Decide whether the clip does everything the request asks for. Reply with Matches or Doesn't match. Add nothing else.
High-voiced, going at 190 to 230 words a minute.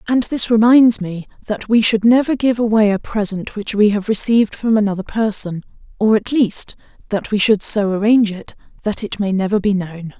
Matches